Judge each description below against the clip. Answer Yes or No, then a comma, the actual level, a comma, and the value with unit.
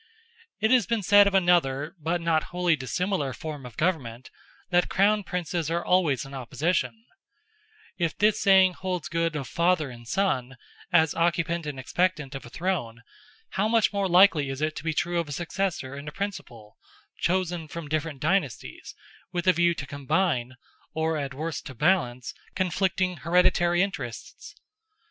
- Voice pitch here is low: No, medium, 170 Hz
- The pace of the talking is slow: No, average, 165 wpm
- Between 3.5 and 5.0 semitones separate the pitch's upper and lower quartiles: Yes, average, 4.6 semitones